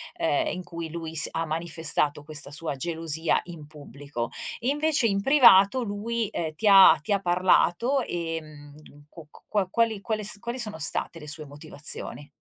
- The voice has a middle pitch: Yes, medium, 170 Hz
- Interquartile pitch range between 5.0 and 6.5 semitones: Yes, wide, 5.6 semitones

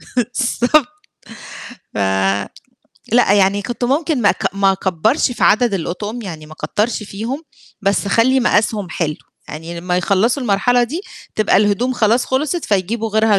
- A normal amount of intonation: Yes, average, 4.0 semitones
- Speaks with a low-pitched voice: No, high, 215 Hz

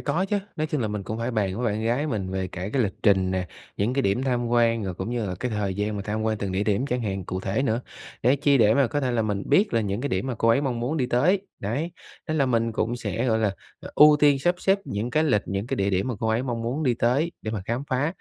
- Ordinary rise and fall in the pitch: Yes, average, 4.5 semitones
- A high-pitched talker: No, low, 115 Hz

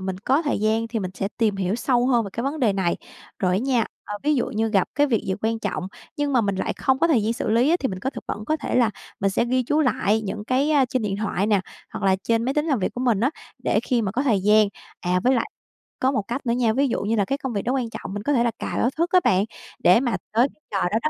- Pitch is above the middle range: Yes, high, 230 Hz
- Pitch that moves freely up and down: No, average, 4.3 semitones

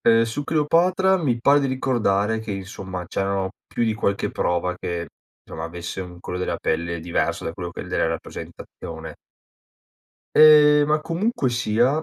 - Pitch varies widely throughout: Yes, wide, 8.4 semitones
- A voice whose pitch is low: Yes, low, 110 Hz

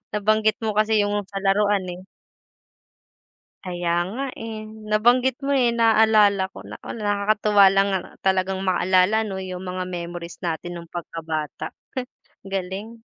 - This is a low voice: No, high, 200 Hz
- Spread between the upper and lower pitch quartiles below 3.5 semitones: Yes, average, 2.9 semitones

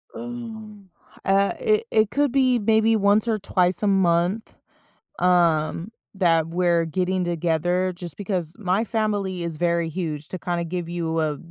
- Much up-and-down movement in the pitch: No, average, 4.0 semitones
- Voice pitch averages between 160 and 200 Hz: Yes, medium, 185 Hz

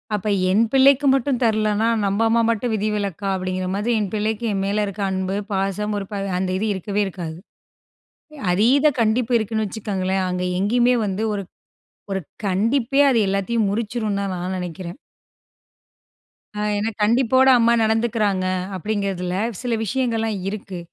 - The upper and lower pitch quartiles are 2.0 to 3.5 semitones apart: Yes, average, 3.0 semitones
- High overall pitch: Yes, high, 210 Hz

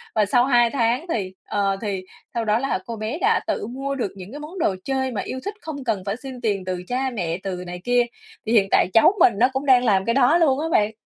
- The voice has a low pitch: No, high, 235 Hz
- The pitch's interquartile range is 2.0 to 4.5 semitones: No, average, 4.9 semitones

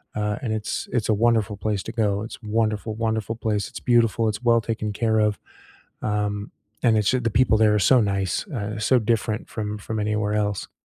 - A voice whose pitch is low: Yes, low, 110 Hz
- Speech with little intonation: Yes, narrow, 1.5 semitones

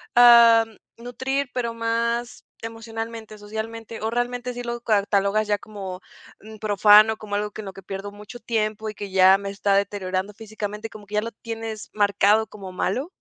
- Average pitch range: No, narrow, 2.0 semitones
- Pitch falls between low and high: No, high, 215 Hz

